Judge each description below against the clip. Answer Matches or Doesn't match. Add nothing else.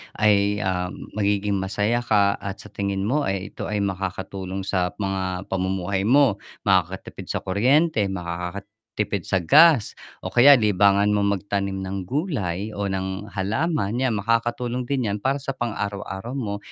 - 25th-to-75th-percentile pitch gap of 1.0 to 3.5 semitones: Matches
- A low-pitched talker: Matches